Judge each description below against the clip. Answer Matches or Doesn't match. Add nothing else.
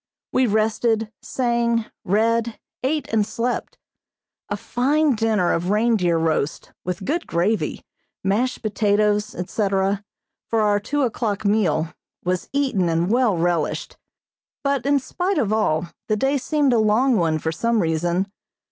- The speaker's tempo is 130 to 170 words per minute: Matches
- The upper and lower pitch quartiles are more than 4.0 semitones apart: Matches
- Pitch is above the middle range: Matches